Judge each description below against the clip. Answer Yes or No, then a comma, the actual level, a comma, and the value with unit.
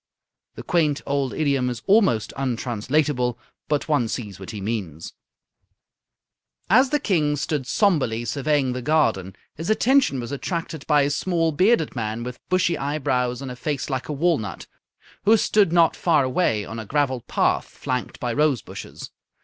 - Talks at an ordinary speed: Yes, average, 160 wpm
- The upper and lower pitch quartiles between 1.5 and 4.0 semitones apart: No, average, 4.7 semitones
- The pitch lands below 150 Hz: Yes, medium, 140 Hz